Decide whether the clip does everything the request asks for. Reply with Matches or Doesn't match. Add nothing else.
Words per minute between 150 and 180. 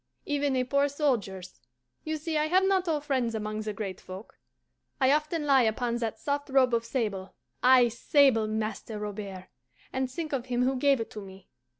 Doesn't match